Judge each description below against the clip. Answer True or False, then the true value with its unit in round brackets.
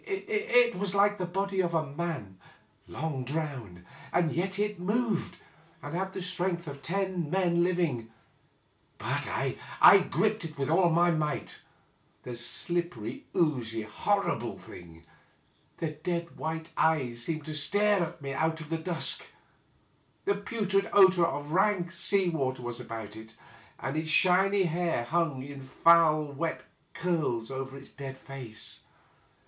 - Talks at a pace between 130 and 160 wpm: True (150 wpm)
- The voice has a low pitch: False (165 Hz)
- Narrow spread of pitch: False (5.3 semitones)